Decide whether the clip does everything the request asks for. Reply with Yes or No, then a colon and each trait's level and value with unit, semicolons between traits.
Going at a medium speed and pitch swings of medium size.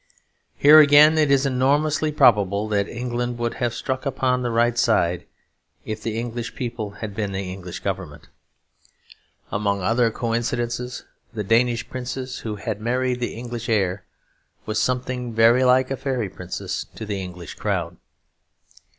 Yes: average, 150 wpm; average, 3.3 semitones